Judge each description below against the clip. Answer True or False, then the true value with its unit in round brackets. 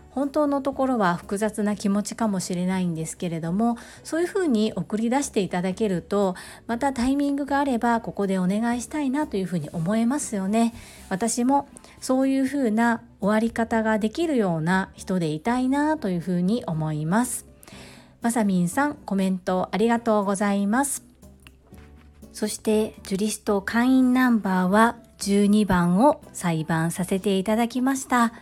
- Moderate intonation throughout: True (4.7 semitones)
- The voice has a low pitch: False (215 Hz)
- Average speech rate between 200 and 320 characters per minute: False (340 characters per minute)